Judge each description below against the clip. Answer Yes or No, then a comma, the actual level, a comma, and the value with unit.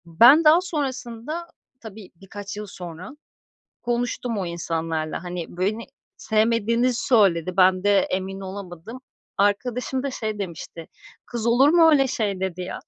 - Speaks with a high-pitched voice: Yes, high, 205 Hz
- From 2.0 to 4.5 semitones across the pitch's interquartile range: No, average, 4.9 semitones